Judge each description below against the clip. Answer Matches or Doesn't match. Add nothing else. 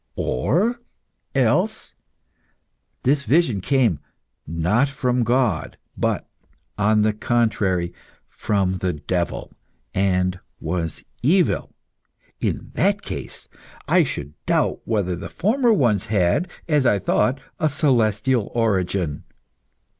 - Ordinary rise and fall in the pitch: Doesn't match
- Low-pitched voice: Matches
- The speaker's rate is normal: Doesn't match